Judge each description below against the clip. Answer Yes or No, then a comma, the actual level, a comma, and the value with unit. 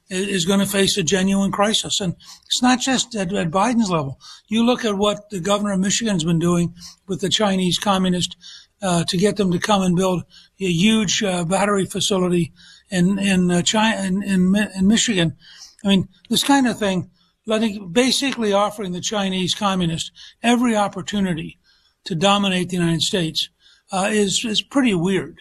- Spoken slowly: No, average, 175 wpm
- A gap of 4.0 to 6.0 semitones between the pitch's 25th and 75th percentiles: No, narrow, 2.5 semitones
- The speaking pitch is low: No, high, 195 Hz